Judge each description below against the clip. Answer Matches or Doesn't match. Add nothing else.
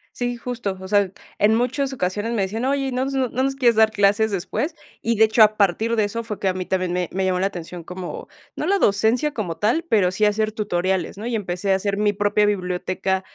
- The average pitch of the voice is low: Doesn't match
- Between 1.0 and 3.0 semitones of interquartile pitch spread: Doesn't match